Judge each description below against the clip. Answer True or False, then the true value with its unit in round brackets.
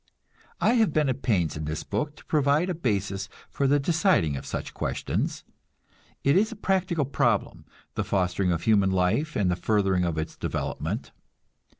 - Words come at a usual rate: True (175 wpm)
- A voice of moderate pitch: False (110 Hz)